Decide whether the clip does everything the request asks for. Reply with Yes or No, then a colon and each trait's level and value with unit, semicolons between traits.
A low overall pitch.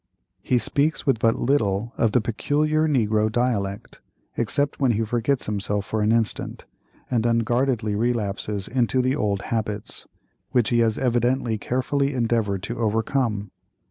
Yes: low, 115 Hz